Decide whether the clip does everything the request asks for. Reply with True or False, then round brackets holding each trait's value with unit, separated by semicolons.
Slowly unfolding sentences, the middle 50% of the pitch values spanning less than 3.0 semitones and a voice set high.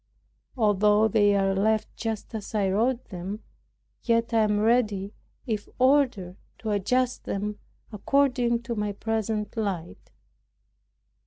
True (125 wpm; 2.4 semitones; 215 Hz)